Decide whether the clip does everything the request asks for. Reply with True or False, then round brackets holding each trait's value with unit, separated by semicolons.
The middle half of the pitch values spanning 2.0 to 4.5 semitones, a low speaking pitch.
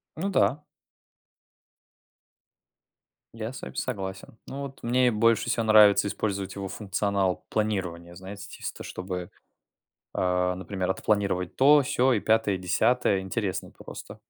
True (3.5 semitones; 100 Hz)